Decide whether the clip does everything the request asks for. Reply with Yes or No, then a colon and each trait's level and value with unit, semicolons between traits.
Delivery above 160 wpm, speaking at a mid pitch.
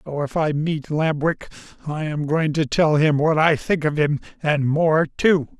Yes: fast, 205 wpm; medium, 155 Hz